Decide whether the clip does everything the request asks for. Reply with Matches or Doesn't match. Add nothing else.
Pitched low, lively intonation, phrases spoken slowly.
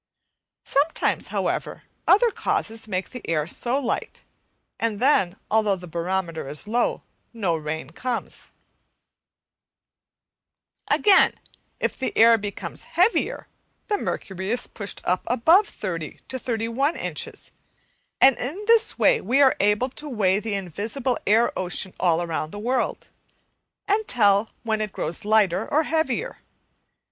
Doesn't match